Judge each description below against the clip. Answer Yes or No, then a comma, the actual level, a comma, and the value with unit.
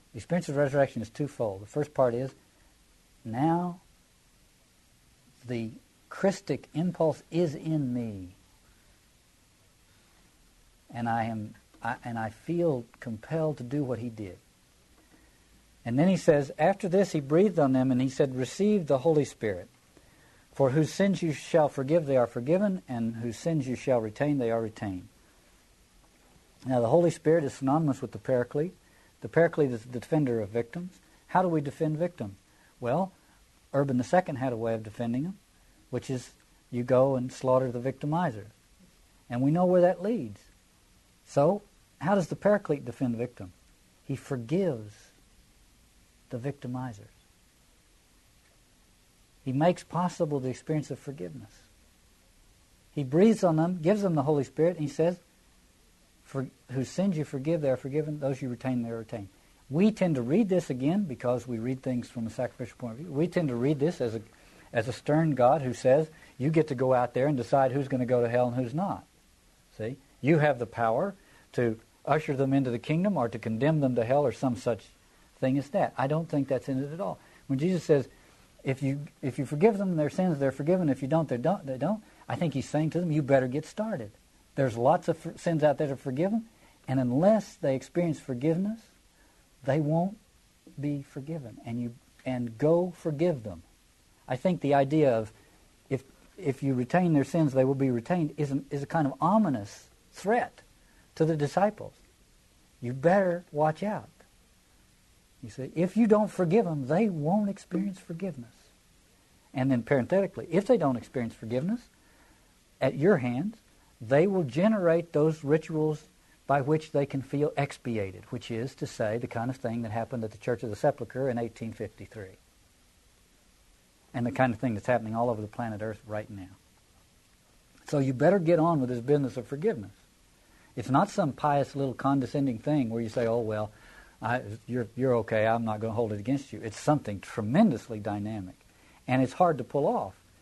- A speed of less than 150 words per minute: No, average, 180 wpm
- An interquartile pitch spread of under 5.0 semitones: No, wide, 5.4 semitones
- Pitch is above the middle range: No, low, 135 Hz